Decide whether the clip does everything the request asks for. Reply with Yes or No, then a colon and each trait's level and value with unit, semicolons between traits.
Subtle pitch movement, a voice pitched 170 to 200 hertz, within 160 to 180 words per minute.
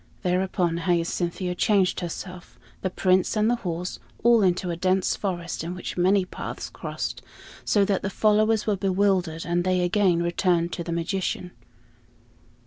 No: narrow, 2.1 semitones; medium, 185 Hz; average, 150 wpm